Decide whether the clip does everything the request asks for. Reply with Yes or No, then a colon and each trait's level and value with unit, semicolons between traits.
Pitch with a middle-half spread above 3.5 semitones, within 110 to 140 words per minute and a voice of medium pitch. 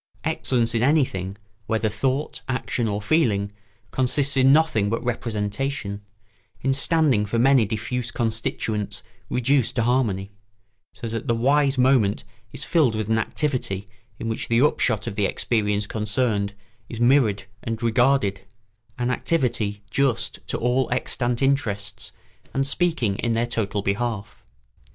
No: average, 4.1 semitones; slow, 135 wpm; low, 115 Hz